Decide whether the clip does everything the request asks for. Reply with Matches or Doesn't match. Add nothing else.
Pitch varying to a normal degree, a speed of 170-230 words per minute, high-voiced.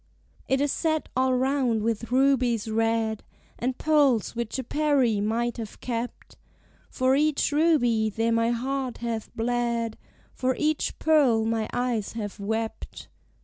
Doesn't match